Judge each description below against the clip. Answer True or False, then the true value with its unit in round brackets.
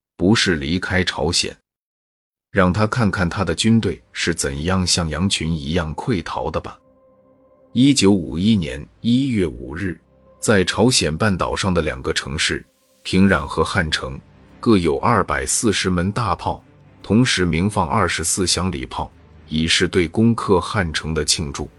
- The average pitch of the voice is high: False (95 Hz)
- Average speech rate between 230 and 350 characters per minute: False (220 characters per minute)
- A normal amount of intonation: True (4.6 semitones)